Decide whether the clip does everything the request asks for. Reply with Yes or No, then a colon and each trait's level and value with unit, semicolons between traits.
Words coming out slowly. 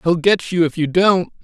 No: fast, 250 wpm